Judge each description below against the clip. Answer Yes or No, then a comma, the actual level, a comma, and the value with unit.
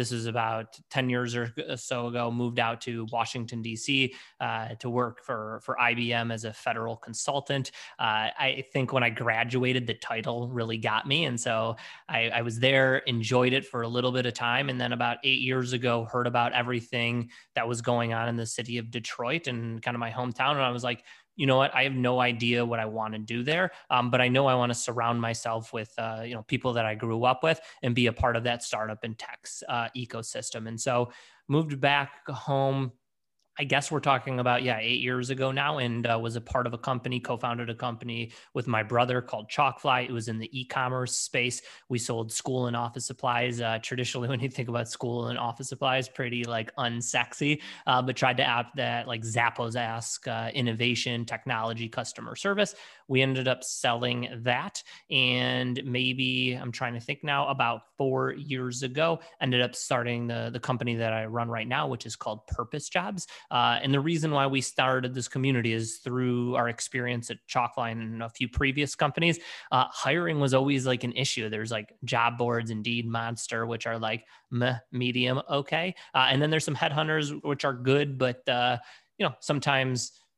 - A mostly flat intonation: Yes, narrow, 2.1 semitones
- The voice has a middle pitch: No, low, 125 Hz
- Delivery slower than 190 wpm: No, fast, 205 wpm